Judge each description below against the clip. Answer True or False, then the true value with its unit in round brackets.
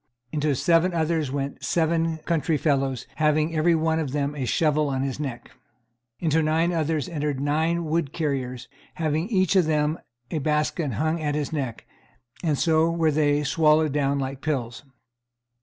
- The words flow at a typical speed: True (160 wpm)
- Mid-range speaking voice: True (155 Hz)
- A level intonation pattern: True (2.3 semitones)